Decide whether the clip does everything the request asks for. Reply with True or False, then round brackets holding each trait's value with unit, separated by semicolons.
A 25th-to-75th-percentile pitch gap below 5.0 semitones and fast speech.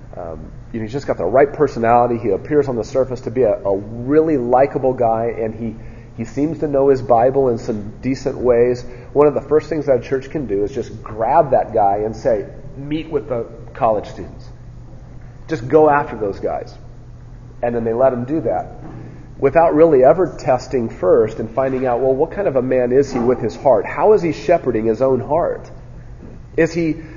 True (3.2 semitones; 210 wpm)